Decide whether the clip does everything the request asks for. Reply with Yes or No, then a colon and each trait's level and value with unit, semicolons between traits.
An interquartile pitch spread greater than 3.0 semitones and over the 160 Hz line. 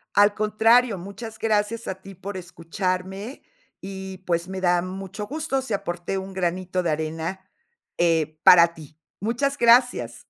Yes: average, 3.5 semitones; high, 190 Hz